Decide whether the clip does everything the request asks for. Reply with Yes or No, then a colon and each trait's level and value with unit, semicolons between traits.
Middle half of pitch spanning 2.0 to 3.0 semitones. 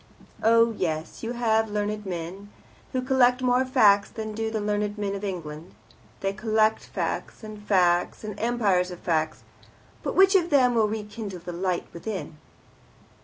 No: average, 3.6 semitones